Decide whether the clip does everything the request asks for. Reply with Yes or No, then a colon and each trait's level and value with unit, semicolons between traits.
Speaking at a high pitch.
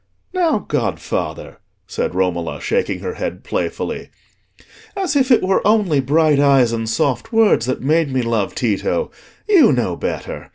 No: medium, 150 Hz